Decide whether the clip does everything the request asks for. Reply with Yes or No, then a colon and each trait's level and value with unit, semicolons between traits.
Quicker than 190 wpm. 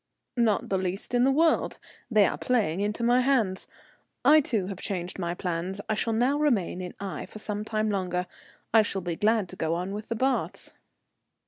Yes: average, 200 wpm